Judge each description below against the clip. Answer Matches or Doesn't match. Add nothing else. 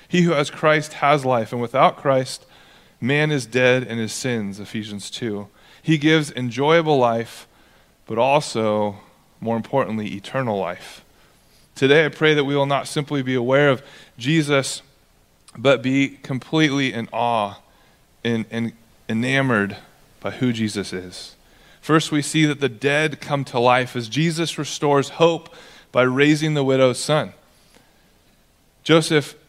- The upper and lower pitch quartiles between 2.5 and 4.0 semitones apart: Doesn't match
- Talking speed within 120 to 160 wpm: Matches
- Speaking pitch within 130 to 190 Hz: Matches